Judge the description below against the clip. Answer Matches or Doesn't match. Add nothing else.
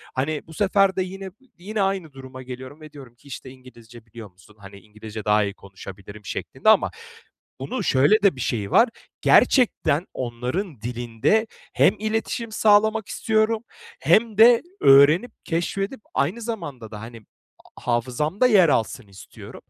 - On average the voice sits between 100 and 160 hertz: Matches